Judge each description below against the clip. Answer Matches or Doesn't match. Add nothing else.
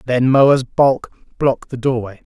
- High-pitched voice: Doesn't match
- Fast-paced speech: Doesn't match